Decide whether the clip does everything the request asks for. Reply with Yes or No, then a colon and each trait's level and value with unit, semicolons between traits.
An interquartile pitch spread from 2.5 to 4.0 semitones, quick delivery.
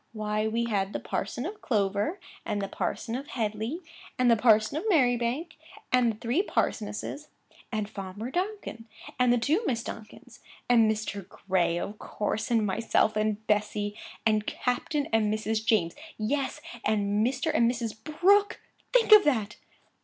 No: average, 3.3 semitones; average, 155 wpm